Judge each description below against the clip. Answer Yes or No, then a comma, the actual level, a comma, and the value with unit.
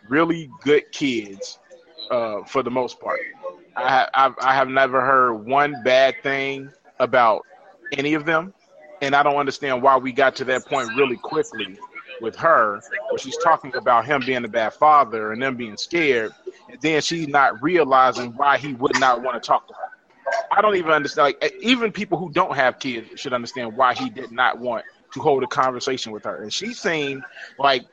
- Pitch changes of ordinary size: No, wide, 5.7 semitones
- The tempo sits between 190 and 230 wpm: Yes, average, 195 wpm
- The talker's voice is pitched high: No, medium, 140 Hz